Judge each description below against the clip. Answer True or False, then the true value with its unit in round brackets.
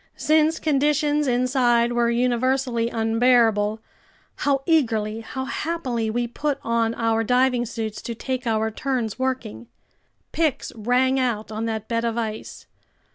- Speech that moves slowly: True (130 wpm)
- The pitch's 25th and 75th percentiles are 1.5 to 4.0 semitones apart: True (2.8 semitones)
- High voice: True (240 Hz)